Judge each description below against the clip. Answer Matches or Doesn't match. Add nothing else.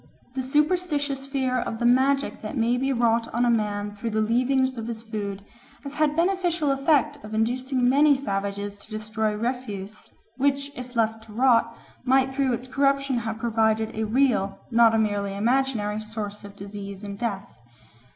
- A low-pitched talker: Doesn't match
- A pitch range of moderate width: Matches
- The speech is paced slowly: Doesn't match